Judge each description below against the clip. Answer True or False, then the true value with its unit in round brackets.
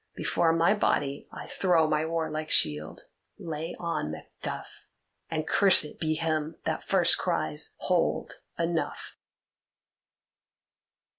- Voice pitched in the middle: True (160 Hz)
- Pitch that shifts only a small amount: True (1.5 semitones)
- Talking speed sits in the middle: False (105 wpm)